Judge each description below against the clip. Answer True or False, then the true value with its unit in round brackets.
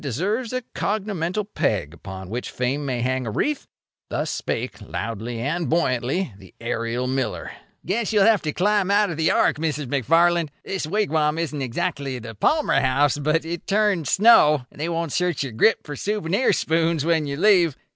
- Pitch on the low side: False (160 Hz)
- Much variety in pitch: True (6.6 semitones)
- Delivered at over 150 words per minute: True (180 wpm)